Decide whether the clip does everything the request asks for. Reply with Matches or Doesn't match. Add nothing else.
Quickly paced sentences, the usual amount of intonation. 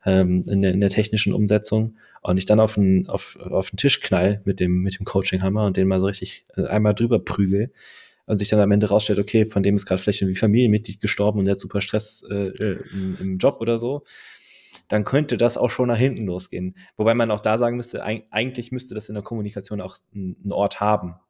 Doesn't match